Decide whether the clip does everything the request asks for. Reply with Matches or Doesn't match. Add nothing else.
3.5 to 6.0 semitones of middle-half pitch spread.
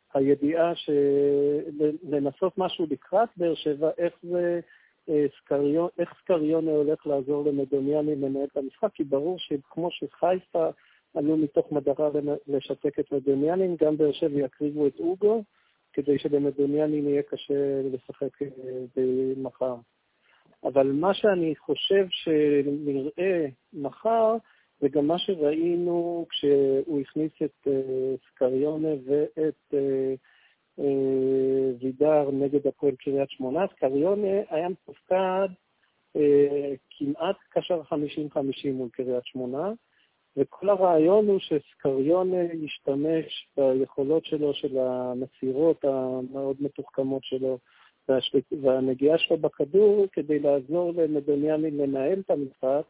Doesn't match